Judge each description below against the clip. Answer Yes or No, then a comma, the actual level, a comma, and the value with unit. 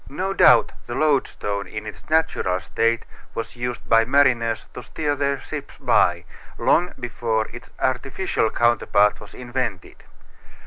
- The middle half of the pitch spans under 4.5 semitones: Yes, average, 4.0 semitones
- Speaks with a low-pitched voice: Yes, low, 120 Hz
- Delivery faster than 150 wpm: No, slow, 135 wpm